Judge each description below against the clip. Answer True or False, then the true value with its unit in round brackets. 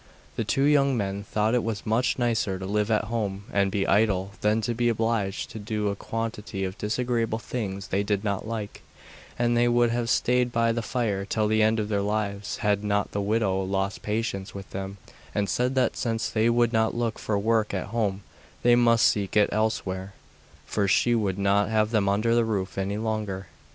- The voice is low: True (105 Hz)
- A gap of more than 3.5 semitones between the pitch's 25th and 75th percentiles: False (2.5 semitones)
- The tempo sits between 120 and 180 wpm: False (205 wpm)